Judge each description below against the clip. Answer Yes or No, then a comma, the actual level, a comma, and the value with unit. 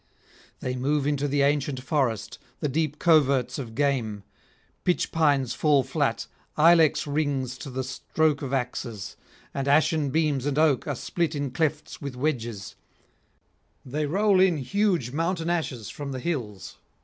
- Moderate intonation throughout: Yes, average, 3.4 semitones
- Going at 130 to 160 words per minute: Yes, average, 150 wpm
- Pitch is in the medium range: Yes, medium, 145 Hz